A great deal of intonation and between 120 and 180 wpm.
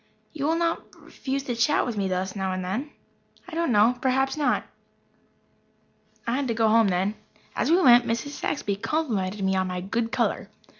No: wide, 6.1 semitones; average, 190 wpm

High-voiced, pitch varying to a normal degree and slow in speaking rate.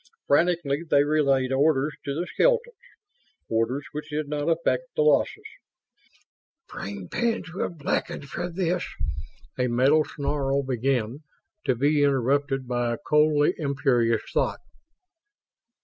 No: medium, 145 Hz; average, 3.0 semitones; slow, 125 wpm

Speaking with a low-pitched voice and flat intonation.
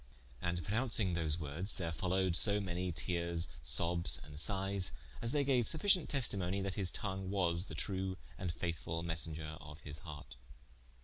No: very low, 90 Hz; average, 3.1 semitones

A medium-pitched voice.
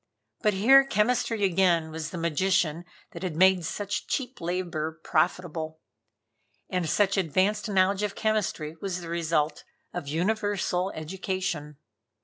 Yes: medium, 180 Hz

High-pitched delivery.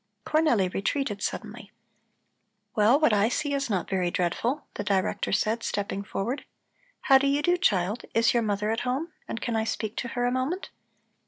Yes: high, 230 Hz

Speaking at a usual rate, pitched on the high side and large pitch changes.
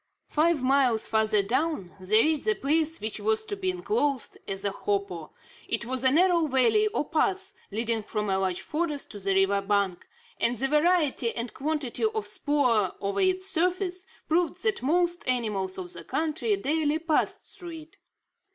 Yes: average, 170 wpm; very high, 285 Hz; wide, 8.3 semitones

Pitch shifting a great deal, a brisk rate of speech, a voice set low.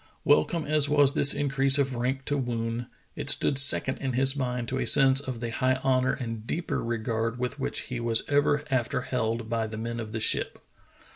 No: average, 2.9 semitones; fast, 210 wpm; low, 130 Hz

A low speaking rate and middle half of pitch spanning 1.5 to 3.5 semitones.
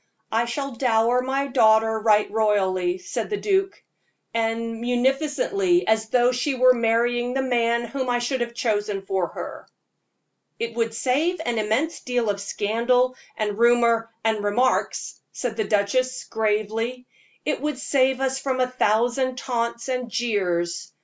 No: average, 150 wpm; average, 2.7 semitones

